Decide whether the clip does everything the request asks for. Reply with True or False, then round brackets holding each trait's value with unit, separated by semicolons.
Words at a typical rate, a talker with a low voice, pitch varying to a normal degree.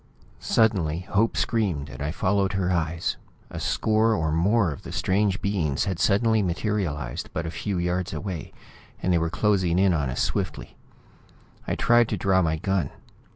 True (170 wpm; 95 Hz; 3.8 semitones)